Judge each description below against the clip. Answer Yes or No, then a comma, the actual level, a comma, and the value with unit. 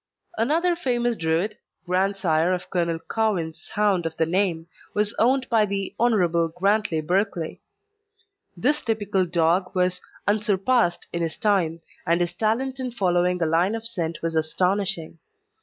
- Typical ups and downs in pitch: Yes, average, 4.5 semitones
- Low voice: No, high, 190 Hz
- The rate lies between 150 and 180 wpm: No, average, 140 wpm